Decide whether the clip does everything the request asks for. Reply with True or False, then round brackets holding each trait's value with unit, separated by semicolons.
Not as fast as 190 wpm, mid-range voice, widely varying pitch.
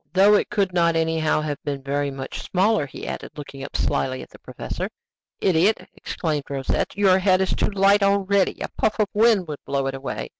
False (195 wpm; 175 Hz; 5.7 semitones)